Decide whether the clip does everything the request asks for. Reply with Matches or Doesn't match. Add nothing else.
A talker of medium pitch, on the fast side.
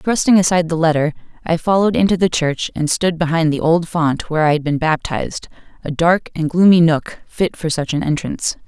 Matches